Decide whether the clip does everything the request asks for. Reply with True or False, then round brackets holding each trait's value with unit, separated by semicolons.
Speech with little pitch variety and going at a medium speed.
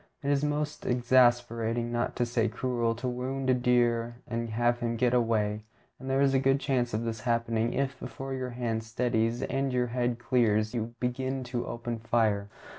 True (1.8 semitones; 190 wpm)